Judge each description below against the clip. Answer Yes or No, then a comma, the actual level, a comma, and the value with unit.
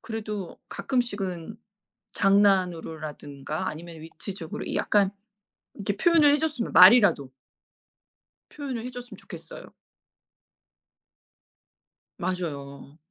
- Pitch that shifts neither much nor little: No, wide, 6.0 semitones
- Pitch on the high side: Yes, high, 195 Hz